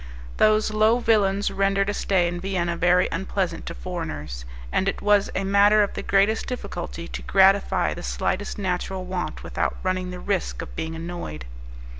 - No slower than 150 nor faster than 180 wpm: Yes, average, 170 wpm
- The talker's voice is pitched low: No, high, 190 Hz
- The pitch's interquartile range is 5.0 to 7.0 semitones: No, narrow, 2.5 semitones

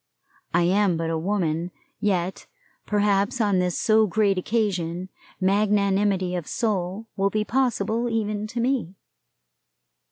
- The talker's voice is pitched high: Yes, high, 200 Hz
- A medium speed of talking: No, slow, 125 wpm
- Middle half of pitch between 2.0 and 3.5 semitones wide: Yes, average, 2.9 semitones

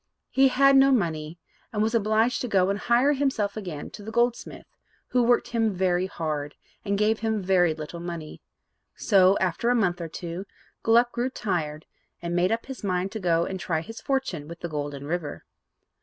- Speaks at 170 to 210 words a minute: Yes, average, 190 wpm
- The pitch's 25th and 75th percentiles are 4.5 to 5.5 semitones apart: Yes, average, 5.2 semitones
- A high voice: Yes, high, 195 Hz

